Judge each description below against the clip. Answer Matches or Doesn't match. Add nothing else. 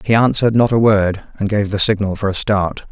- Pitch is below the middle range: Matches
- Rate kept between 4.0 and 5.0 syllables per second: Doesn't match